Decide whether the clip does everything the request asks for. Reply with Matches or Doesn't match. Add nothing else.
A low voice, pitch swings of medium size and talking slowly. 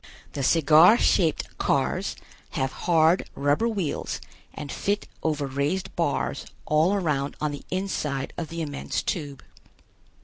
Doesn't match